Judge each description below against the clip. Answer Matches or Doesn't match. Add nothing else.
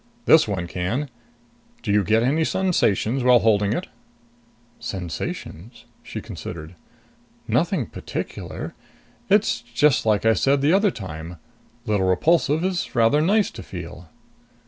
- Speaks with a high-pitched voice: Doesn't match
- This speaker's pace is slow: Matches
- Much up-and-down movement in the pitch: Matches